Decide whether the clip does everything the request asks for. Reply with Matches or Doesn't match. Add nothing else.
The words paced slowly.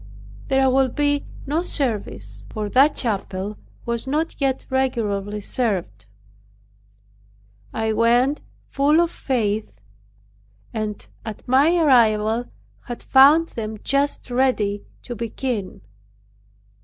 Matches